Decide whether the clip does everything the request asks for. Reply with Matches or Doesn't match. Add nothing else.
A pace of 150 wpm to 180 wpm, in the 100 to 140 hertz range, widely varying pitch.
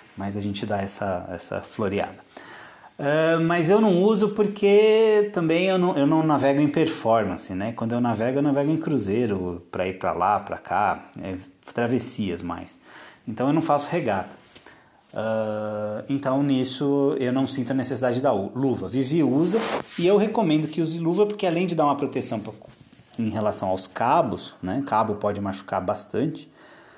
Matches